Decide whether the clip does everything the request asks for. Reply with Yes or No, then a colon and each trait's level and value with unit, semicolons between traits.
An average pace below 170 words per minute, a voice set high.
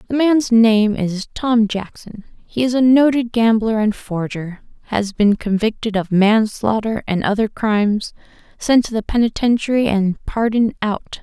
Yes: average, 150 wpm; high, 220 Hz